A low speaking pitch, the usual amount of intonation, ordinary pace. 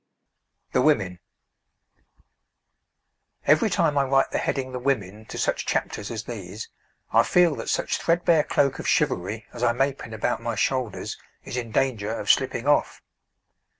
Yes: low, 125 Hz; average, 4.0 semitones; average, 155 wpm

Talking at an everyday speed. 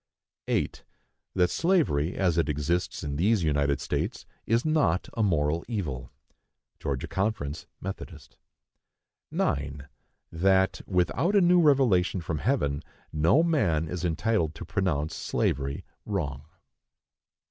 No: slow, 115 wpm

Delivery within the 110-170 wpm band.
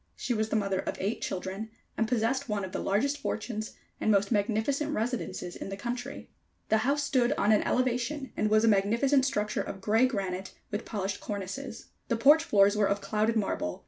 No: average, 195 wpm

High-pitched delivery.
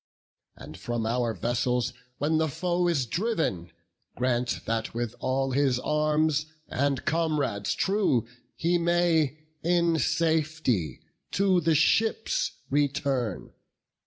No: medium, 145 Hz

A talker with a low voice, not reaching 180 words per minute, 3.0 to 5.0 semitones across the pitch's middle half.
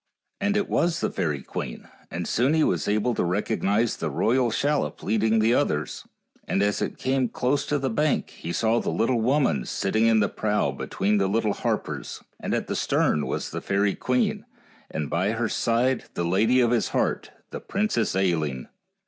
No: low, 110 Hz; average, 190 wpm; average, 4.6 semitones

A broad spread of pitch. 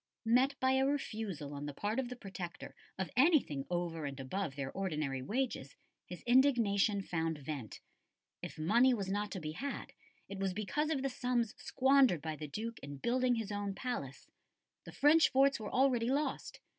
Yes: wide, 8.1 semitones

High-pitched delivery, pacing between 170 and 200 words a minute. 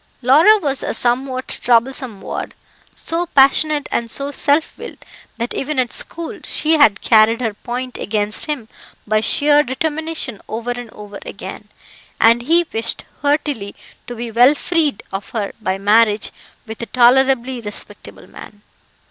No: high, 245 Hz; average, 150 wpm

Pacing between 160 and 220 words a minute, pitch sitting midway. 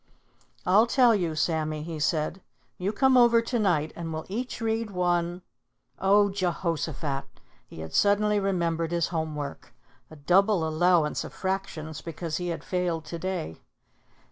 No: average, 150 wpm; medium, 175 Hz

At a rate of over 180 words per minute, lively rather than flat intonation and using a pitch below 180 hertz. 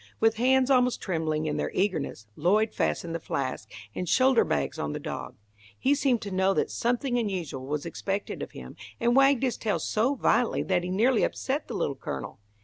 No: average, 195 wpm; wide, 7.5 semitones; high, 205 Hz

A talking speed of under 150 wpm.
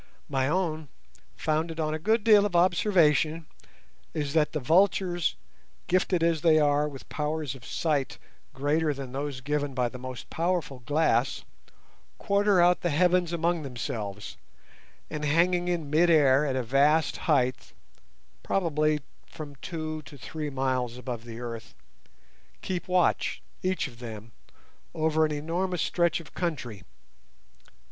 Yes: slow, 135 wpm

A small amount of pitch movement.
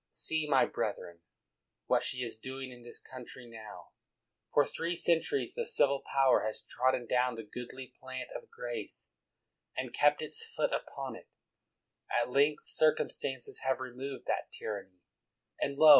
No: average, 4.1 semitones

